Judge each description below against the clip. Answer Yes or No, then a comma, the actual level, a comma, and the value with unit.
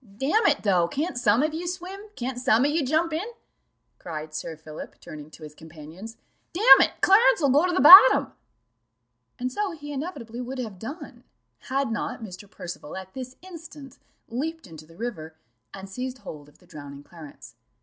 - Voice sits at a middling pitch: No, very high, 250 Hz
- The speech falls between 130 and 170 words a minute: No, average, 180 wpm